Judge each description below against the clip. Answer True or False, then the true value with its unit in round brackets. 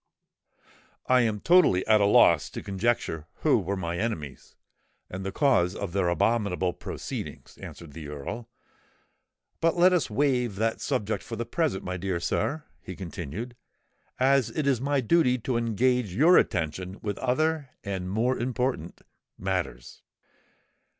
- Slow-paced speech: False (145 wpm)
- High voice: False (110 Hz)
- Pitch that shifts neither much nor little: False (5.8 semitones)